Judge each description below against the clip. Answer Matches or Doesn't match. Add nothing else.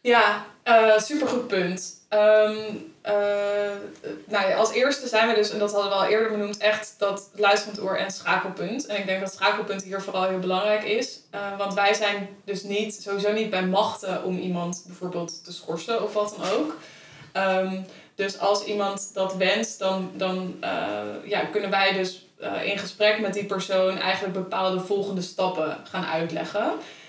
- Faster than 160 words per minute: Matches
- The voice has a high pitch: Matches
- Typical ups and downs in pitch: Doesn't match